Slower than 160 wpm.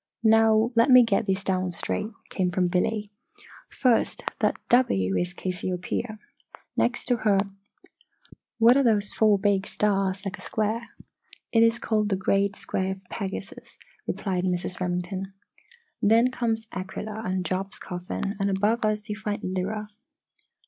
Yes: average, 145 wpm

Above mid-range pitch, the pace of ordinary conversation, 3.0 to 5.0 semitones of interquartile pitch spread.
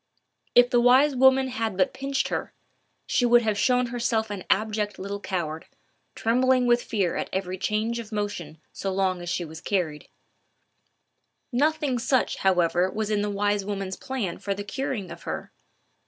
Yes: high, 210 Hz; average, 170 wpm; average, 4.5 semitones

